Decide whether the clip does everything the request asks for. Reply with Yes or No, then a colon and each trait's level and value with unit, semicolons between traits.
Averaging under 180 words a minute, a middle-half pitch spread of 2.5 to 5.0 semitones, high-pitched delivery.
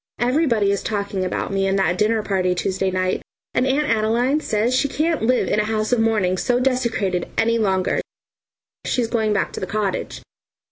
No: average, 185 wpm; average, 4.0 semitones; high, 215 Hz